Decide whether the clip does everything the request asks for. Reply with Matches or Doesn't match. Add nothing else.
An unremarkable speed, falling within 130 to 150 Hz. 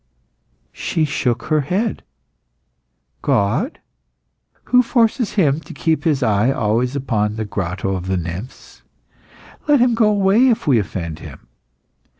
Doesn't match